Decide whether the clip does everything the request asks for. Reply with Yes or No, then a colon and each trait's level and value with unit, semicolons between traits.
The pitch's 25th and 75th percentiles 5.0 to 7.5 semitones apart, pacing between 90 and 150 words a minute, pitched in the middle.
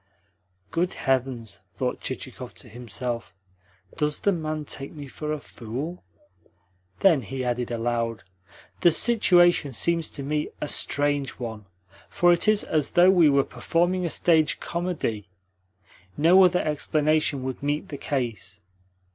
Yes: wide, 5.4 semitones; average, 140 wpm; medium, 145 Hz